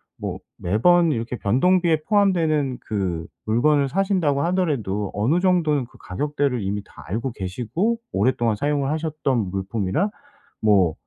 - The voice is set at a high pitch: No, low, 135 Hz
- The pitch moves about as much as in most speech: No, wide, 7.7 semitones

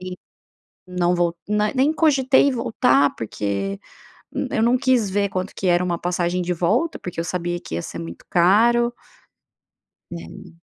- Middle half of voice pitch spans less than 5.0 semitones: No, average, 5.3 semitones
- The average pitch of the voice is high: No, medium, 180 Hz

